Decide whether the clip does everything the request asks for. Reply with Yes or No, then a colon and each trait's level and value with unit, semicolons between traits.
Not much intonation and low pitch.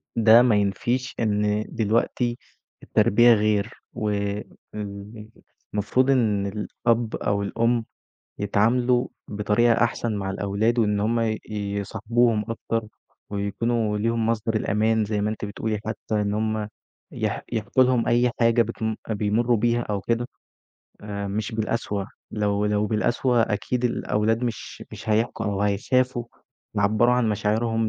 Yes: narrow, 2.1 semitones; low, 110 Hz